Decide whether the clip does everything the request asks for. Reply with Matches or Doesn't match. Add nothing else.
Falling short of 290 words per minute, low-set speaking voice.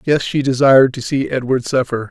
Matches